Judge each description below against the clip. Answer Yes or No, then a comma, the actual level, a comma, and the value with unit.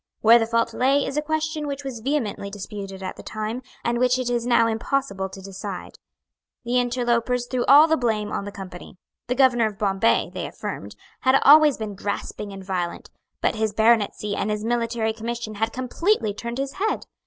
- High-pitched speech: Yes, high, 230 Hz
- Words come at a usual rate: Yes, average, 190 wpm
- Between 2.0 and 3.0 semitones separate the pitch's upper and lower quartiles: No, average, 3.8 semitones